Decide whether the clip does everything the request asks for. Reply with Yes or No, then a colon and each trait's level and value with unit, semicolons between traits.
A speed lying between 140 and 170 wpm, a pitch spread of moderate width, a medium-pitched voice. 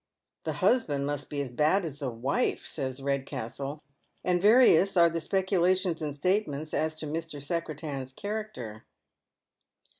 Yes: average, 145 wpm; average, 4.4 semitones; medium, 155 Hz